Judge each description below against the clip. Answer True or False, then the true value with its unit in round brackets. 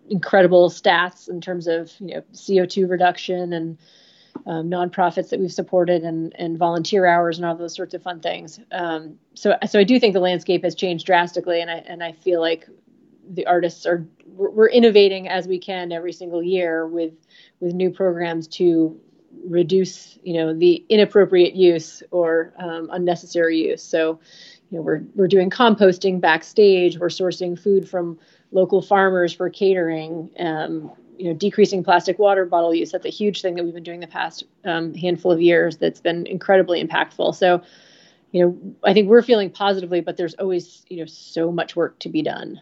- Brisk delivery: False (180 wpm)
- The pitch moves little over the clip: True (2.0 semitones)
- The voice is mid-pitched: True (175 Hz)